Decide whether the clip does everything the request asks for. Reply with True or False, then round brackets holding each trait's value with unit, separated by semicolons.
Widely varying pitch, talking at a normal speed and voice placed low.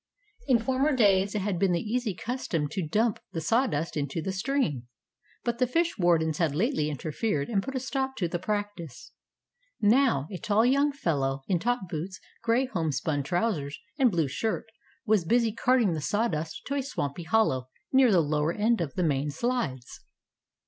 False (7.2 semitones; 175 wpm; 195 Hz)